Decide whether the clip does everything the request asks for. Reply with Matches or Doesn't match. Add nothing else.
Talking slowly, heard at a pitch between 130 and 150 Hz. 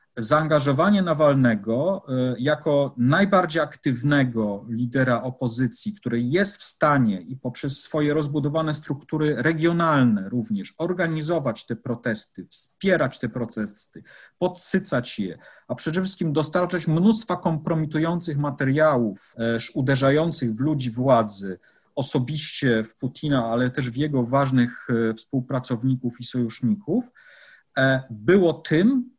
Matches